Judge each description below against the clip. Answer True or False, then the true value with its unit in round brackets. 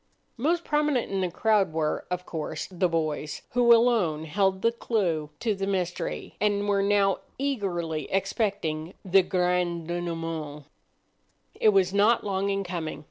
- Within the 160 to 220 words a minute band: False (145 wpm)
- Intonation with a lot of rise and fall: False (3.7 semitones)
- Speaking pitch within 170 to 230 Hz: True (190 Hz)